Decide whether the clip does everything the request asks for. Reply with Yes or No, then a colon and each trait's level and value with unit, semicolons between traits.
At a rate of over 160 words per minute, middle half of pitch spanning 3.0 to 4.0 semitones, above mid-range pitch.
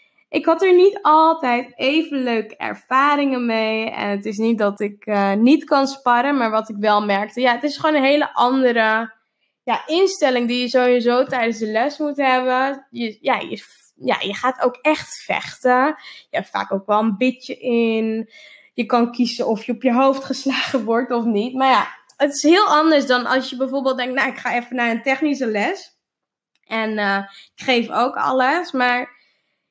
Yes: average, 195 wpm; average, 3.3 semitones; very high, 250 Hz